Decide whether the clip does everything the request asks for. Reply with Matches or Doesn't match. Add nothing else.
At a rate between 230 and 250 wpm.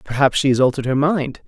Matches